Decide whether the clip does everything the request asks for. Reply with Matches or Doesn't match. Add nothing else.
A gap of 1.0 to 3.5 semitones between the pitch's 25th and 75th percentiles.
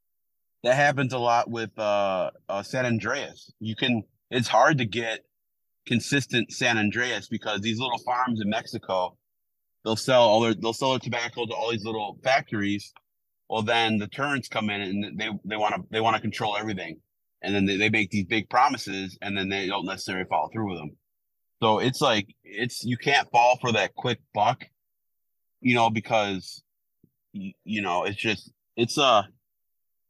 Matches